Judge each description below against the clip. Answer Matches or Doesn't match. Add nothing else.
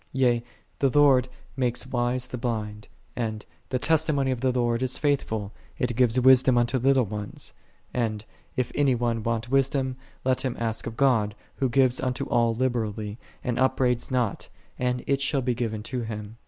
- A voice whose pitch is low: Matches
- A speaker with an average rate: Matches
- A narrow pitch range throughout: Matches